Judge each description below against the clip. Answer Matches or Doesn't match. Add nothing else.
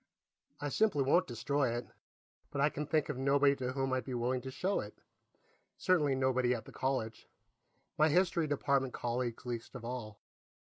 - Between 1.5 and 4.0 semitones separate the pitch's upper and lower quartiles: Matches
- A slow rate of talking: Doesn't match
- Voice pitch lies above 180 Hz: Doesn't match